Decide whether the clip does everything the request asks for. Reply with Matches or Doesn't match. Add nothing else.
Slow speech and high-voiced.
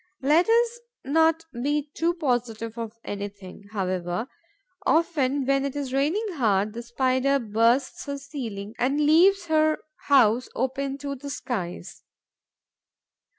Matches